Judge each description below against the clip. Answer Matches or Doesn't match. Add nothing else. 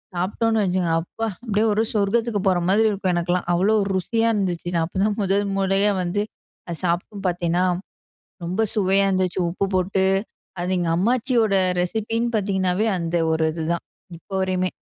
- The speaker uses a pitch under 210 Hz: Matches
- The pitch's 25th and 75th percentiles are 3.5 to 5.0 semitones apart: Doesn't match